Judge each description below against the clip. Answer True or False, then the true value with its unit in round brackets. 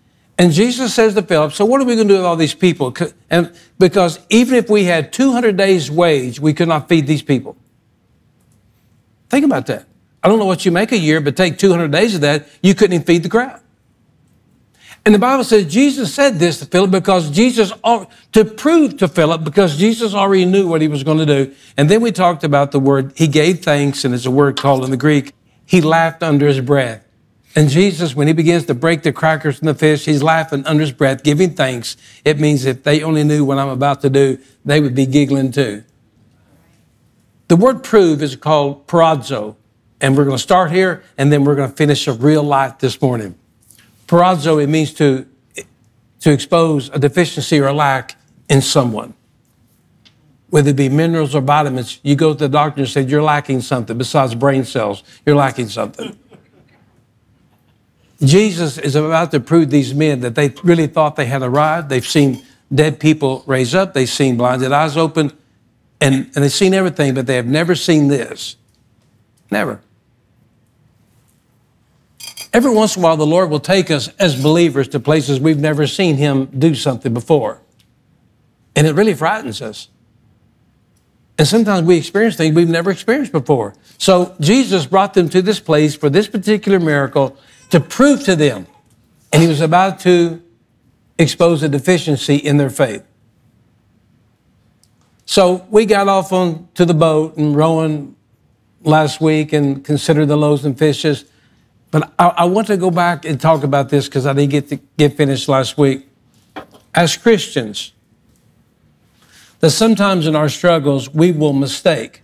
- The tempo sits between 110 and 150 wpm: False (180 wpm)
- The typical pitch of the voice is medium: True (150 Hz)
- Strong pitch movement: False (4.3 semitones)